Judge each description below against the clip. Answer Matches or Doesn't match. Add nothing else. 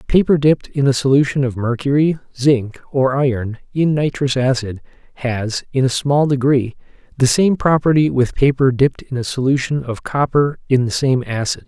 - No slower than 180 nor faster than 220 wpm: Doesn't match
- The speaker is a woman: Doesn't match